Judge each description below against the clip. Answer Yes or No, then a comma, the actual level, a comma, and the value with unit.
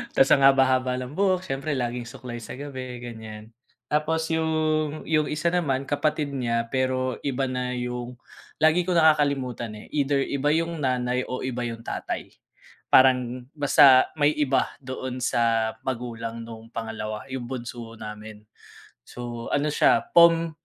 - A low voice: Yes, low, 130 Hz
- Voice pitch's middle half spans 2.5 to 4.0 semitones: Yes, average, 3.4 semitones